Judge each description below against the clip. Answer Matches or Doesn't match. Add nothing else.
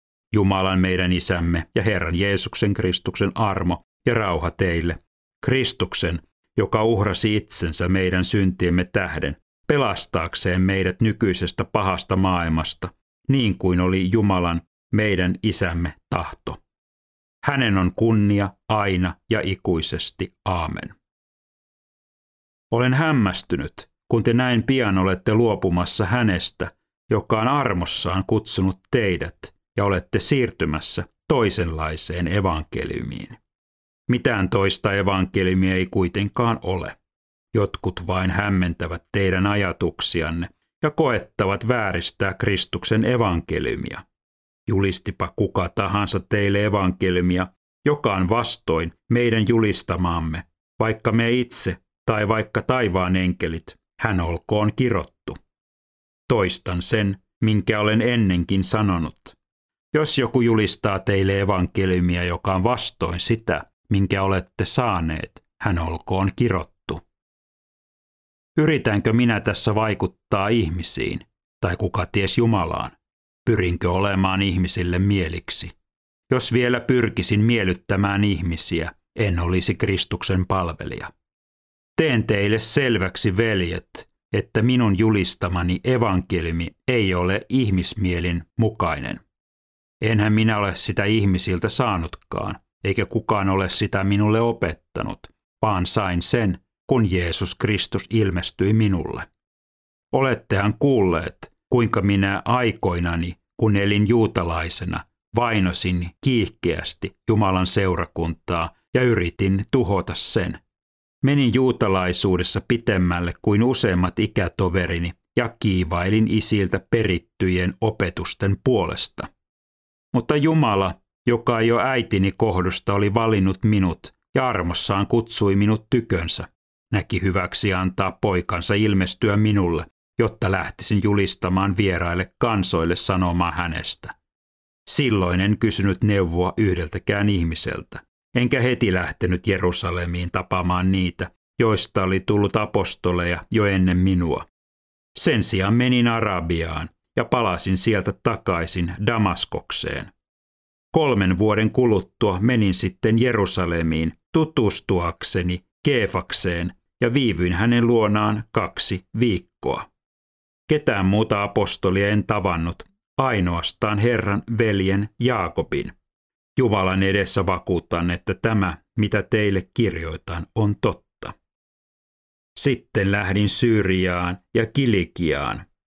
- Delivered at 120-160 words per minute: Doesn't match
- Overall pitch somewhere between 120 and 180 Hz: Doesn't match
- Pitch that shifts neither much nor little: Matches